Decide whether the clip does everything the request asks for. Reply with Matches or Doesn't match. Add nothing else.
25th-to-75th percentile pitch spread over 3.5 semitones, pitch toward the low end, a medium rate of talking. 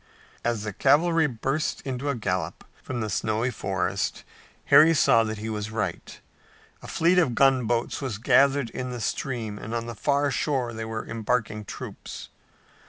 Matches